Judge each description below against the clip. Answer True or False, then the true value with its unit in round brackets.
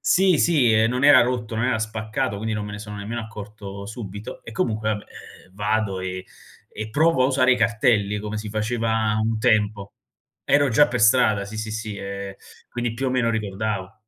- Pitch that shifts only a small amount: True (2.3 semitones)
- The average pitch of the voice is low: True (110 Hz)